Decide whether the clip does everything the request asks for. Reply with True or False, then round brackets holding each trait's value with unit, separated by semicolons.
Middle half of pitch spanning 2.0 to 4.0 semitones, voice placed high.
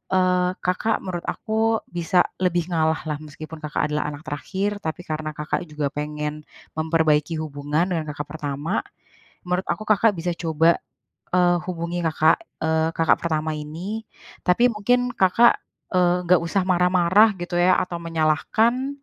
False (2.9 semitones; 170 Hz)